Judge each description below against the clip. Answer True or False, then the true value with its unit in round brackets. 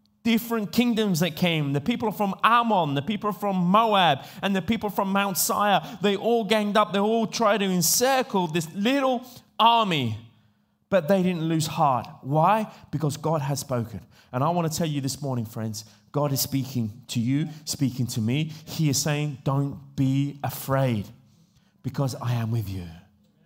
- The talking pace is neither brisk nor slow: False (175 wpm)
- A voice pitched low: False (160 Hz)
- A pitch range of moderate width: False (7.6 semitones)